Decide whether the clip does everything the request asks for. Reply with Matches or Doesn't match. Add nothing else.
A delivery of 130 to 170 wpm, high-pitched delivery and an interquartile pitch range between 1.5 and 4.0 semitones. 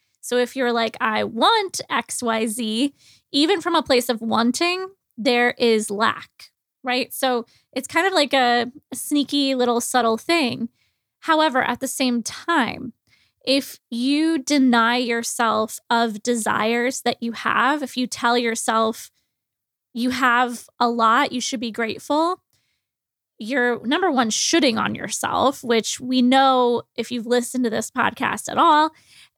Matches